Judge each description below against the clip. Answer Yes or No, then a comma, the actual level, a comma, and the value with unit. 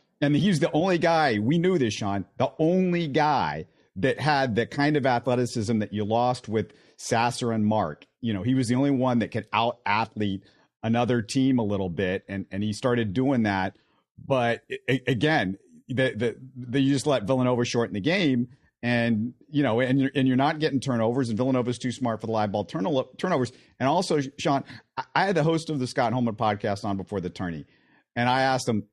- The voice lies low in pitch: Yes, low, 125 Hz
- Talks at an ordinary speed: No, fast, 210 wpm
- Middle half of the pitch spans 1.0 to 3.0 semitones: No, average, 3.6 semitones